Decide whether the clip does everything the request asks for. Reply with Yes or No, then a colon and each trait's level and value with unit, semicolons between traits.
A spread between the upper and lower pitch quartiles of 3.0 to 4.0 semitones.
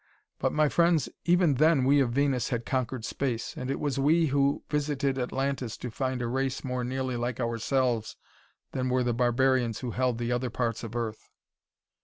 No: narrow, 2.4 semitones